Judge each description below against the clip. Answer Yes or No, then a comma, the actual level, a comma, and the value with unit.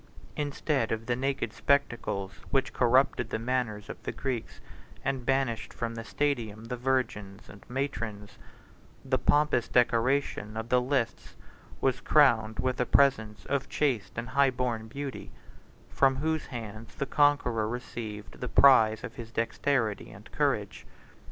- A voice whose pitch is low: Yes, low, 125 Hz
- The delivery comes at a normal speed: Yes, average, 145 wpm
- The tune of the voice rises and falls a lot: No, average, 3.4 semitones